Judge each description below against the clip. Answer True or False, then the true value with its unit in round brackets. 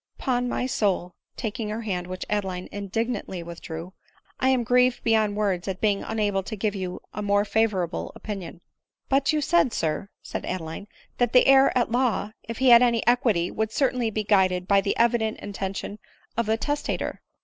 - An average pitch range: True (3.9 semitones)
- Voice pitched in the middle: False (215 Hz)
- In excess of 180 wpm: True (190 wpm)